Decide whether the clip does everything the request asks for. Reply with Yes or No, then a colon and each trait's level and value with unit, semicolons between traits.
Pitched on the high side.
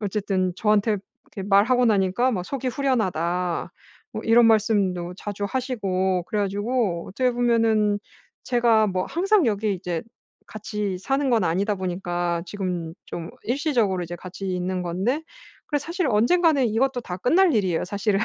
Yes: high, 205 Hz